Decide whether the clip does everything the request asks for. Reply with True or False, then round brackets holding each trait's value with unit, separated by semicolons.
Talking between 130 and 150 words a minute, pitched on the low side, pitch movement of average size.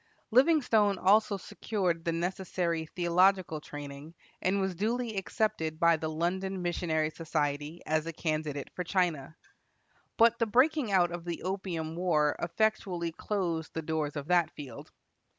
False (140 wpm; 175 Hz; 3.6 semitones)